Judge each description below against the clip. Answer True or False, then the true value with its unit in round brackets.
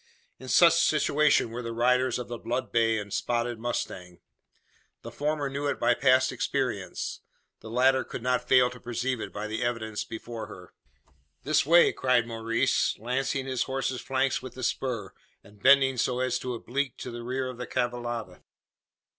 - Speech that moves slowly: False (175 wpm)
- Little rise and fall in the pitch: True (2.1 semitones)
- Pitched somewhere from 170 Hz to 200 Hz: False (125 Hz)